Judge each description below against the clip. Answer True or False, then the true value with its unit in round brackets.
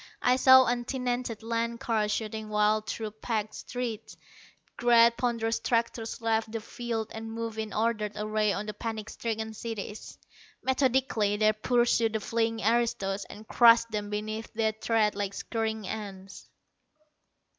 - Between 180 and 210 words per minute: False (140 wpm)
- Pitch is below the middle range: False (225 Hz)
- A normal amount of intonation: False (1.6 semitones)